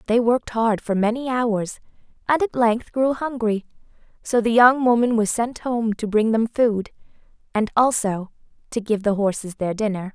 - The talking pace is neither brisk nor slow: Yes, average, 175 wpm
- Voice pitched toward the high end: Yes, high, 225 Hz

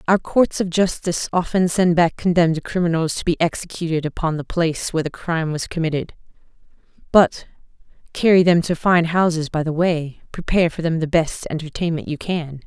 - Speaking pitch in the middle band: Yes, medium, 165 Hz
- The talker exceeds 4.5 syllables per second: Yes, 5.6 syllables/s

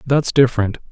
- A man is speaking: Yes, male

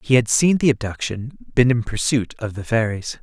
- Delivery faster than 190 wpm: Yes, fast, 205 wpm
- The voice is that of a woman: No, male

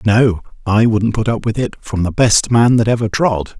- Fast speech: Yes, fast, 235 wpm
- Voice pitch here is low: Yes, low, 110 Hz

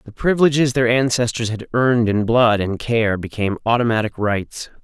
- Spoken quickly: No, average, 160 wpm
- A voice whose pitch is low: Yes, low, 115 Hz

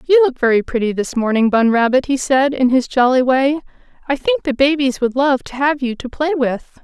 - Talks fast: Yes, fast, 230 wpm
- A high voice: Yes, very high, 265 Hz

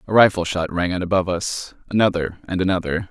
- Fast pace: No, average, 195 wpm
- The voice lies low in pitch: Yes, very low, 90 Hz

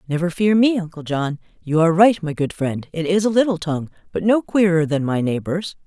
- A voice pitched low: No, medium, 170 Hz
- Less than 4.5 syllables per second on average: No, 5.6 syllables/s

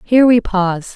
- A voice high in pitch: Yes, high, 210 Hz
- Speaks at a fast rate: No, average, 190 wpm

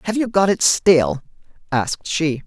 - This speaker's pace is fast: No, average, 170 wpm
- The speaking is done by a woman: No, male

